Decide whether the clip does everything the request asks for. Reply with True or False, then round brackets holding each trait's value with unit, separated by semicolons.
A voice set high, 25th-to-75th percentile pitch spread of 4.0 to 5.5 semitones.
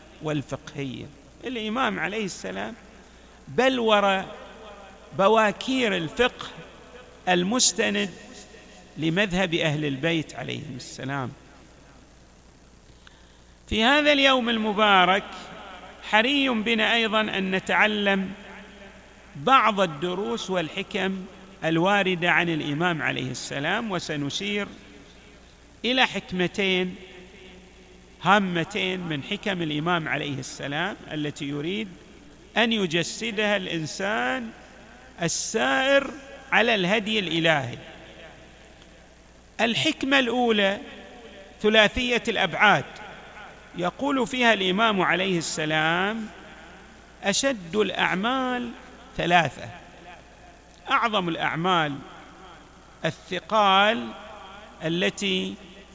True (195 Hz; 4.5 semitones)